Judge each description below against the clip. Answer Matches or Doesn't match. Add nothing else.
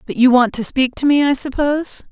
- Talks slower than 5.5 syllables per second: Doesn't match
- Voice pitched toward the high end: Matches